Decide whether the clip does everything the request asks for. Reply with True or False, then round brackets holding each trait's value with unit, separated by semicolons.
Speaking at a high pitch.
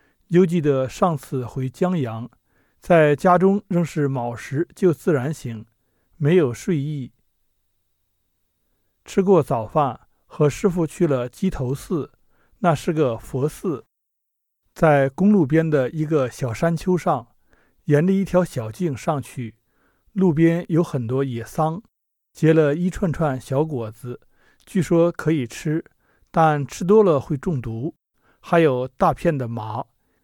False (150 Hz)